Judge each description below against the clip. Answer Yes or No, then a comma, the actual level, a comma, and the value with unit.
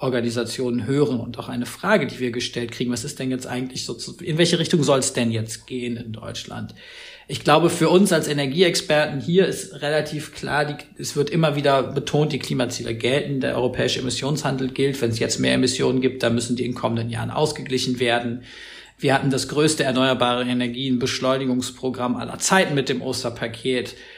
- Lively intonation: No, average, 3.2 semitones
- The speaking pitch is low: Yes, low, 130 Hz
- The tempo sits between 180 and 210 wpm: Yes, average, 185 wpm